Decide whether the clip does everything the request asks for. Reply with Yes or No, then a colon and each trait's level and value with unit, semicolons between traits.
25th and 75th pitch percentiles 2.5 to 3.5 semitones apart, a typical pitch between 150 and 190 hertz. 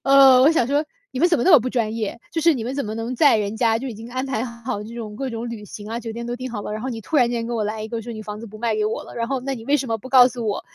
No: average, 2.8 semitones; high, 235 Hz